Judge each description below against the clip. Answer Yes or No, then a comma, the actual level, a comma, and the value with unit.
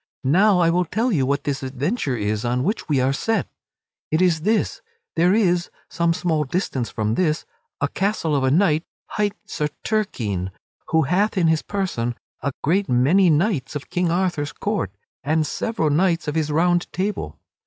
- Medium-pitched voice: Yes, medium, 165 Hz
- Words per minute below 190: Yes, average, 175 wpm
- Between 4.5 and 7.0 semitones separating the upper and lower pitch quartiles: Yes, average, 5.2 semitones